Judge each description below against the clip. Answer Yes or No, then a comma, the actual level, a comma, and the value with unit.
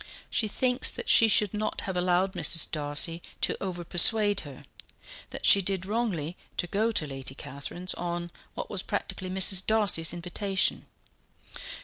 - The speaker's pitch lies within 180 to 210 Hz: Yes, medium, 185 Hz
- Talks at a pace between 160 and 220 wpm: No, average, 150 wpm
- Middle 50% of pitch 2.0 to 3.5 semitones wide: Yes, average, 3.2 semitones